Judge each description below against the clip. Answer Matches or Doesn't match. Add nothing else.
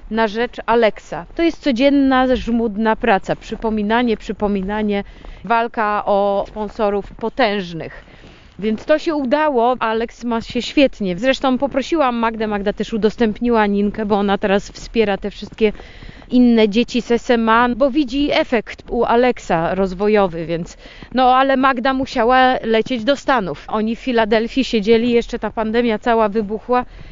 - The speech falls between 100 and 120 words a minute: Doesn't match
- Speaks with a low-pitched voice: Doesn't match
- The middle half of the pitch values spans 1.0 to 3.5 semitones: Matches